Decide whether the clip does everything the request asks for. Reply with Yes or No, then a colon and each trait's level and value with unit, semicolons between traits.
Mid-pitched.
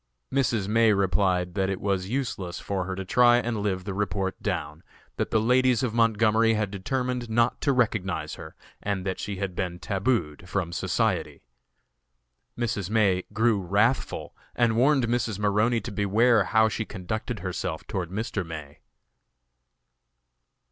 No: low, 105 Hz